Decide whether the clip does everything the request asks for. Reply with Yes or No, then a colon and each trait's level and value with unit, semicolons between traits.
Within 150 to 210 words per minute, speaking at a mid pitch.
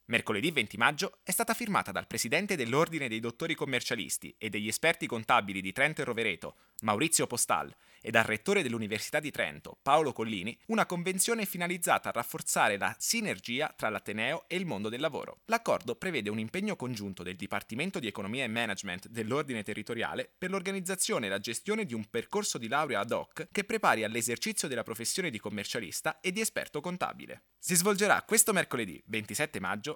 Yes: fast, 170 wpm; medium, 150 Hz